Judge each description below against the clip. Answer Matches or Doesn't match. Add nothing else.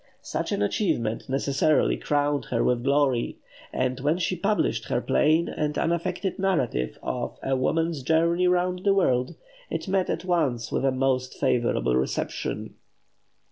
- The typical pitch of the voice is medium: Matches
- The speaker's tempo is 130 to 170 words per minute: Matches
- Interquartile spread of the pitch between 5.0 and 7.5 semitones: Matches